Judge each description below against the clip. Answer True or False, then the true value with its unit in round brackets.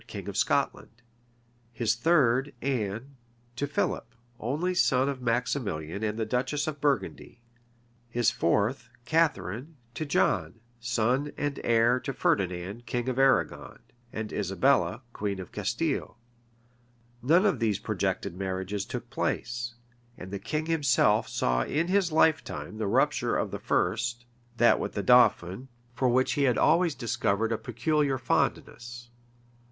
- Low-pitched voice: True (120 Hz)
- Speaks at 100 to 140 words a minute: True (135 wpm)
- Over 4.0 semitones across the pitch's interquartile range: True (4.4 semitones)